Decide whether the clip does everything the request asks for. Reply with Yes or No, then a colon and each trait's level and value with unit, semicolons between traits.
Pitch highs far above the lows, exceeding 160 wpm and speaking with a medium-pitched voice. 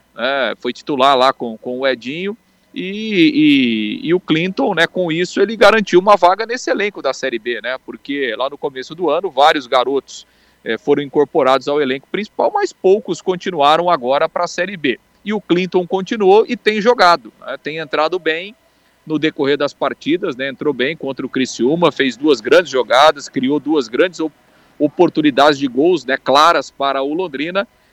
Yes: wide, 5.7 semitones; average, 180 wpm; medium, 170 Hz